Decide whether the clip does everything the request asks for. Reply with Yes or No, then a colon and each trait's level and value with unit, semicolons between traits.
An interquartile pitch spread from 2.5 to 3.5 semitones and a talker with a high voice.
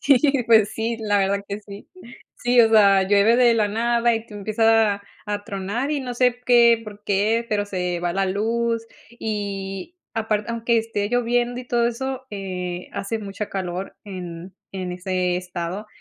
Yes: average, 3.1 semitones; high, 210 Hz